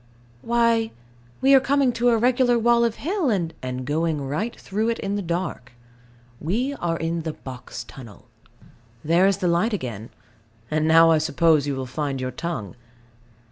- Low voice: No, medium, 170 Hz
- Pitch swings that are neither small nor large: No, wide, 7.8 semitones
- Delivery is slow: No, average, 175 wpm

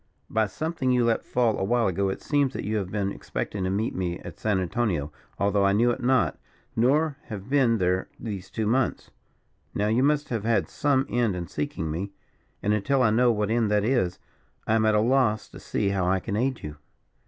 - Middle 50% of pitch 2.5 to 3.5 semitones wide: No, average, 3.9 semitones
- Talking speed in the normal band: No, fast, 220 wpm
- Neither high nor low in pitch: No, low, 110 Hz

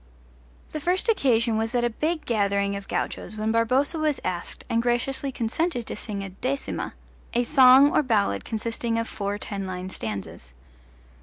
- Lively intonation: No, average, 4.9 semitones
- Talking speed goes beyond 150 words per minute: Yes, average, 165 wpm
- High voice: Yes, high, 230 Hz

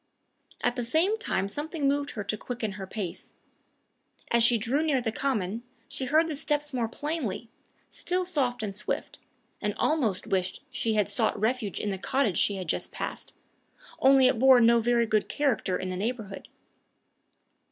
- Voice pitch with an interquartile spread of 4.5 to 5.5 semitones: Yes, average, 5.0 semitones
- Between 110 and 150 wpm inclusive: No, average, 175 wpm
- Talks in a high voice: Yes, high, 235 Hz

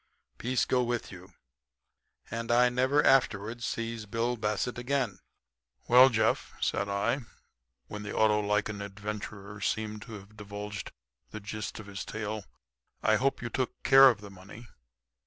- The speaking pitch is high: No, low, 110 Hz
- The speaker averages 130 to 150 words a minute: Yes, average, 145 wpm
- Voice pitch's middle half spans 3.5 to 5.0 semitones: No, average, 2.8 semitones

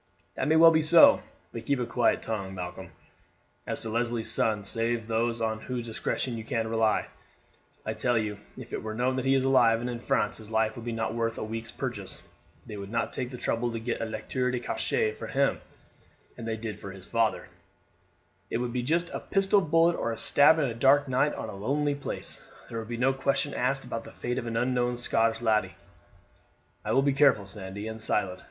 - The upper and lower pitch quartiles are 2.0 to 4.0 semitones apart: Yes, average, 2.9 semitones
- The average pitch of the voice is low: Yes, low, 115 Hz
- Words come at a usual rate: No, fast, 225 wpm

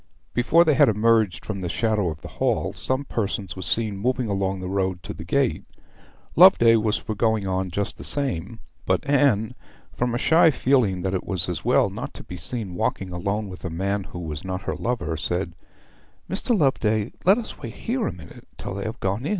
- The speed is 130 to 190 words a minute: No, average, 200 wpm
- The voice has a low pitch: Yes, low, 105 Hz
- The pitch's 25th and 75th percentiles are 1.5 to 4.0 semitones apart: No, average, 4.5 semitones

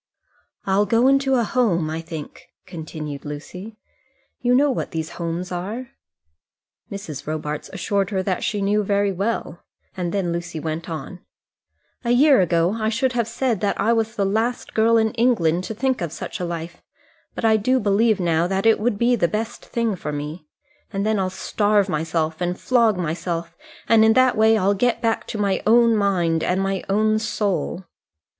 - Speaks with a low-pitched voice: No, high, 200 Hz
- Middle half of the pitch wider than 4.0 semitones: Yes, average, 4.7 semitones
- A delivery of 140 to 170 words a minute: No, average, 180 wpm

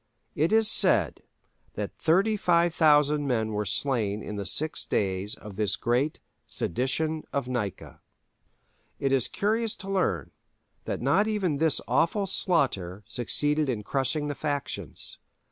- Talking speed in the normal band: No, slow, 130 wpm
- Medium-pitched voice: Yes, medium, 145 Hz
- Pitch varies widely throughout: Yes, wide, 7.2 semitones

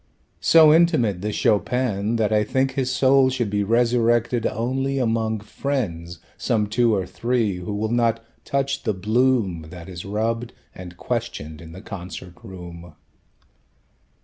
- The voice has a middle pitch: No, low, 110 Hz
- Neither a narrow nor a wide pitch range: Yes, average, 4.5 semitones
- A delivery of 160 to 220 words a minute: No, average, 145 wpm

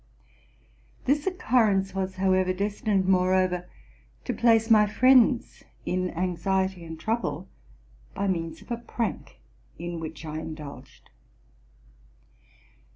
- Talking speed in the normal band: No, slow, 105 wpm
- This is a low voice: No, high, 190 Hz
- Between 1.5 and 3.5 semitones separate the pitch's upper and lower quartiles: No, average, 4.1 semitones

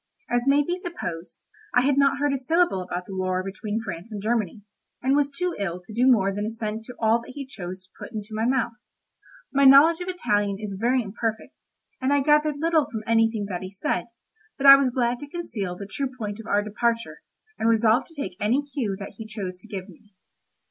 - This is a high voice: Yes, high, 225 Hz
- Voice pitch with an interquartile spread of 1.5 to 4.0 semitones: No, average, 5.3 semitones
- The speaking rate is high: Yes, fast, 220 wpm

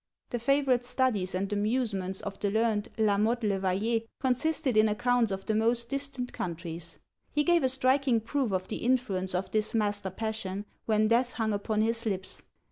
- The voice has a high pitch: Yes, high, 220 Hz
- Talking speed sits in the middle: Yes, average, 180 wpm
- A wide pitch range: No, average, 3.7 semitones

